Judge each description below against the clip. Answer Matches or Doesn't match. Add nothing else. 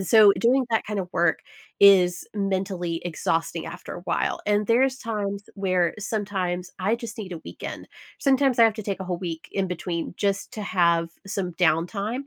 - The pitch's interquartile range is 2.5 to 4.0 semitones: Matches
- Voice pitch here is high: Matches